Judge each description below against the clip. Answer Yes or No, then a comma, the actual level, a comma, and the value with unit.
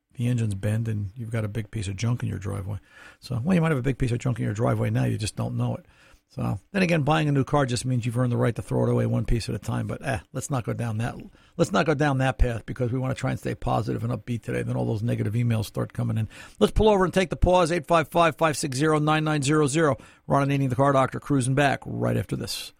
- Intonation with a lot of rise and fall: No, average, 4.9 semitones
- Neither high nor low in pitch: No, low, 125 Hz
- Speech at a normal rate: No, fast, 280 wpm